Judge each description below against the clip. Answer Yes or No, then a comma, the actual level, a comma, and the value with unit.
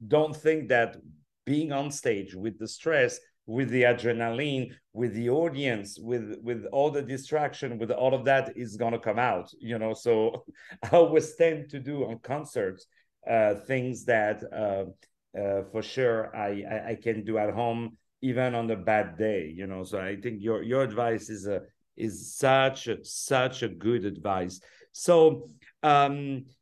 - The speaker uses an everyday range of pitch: Yes, average, 4.3 semitones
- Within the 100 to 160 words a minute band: No, average, 170 wpm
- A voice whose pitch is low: Yes, low, 120 Hz